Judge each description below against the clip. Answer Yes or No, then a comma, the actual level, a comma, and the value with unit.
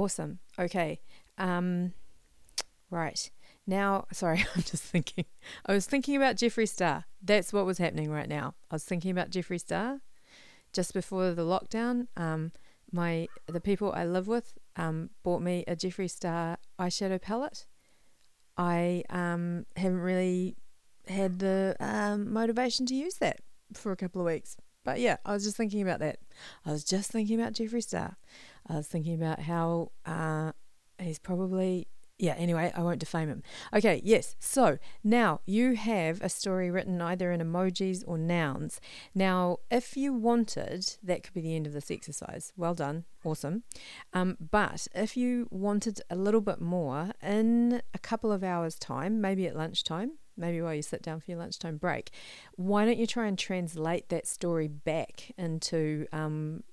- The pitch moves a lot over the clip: No, average, 3.6 semitones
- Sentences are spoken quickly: No, average, 165 wpm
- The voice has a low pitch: No, medium, 180 Hz